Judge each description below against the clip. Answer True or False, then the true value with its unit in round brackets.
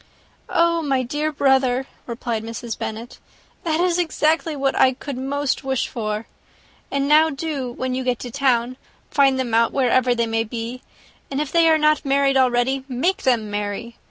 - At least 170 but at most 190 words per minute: True (175 wpm)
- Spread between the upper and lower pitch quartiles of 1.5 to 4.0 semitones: True (3.3 semitones)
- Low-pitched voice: False (260 Hz)